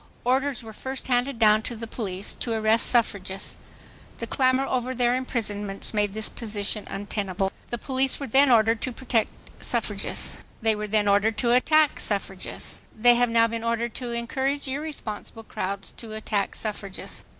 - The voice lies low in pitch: No, high, 230 Hz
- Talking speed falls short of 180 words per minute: Yes, average, 160 wpm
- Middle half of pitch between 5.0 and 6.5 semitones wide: No, average, 3.2 semitones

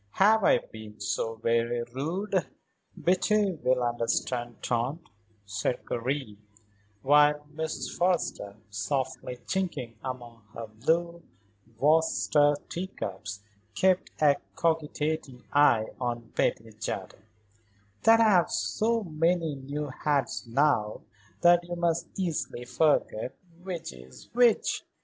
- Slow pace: Yes, slow, 110 wpm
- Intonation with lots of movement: Yes, wide, 6.3 semitones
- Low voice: No, medium, 145 Hz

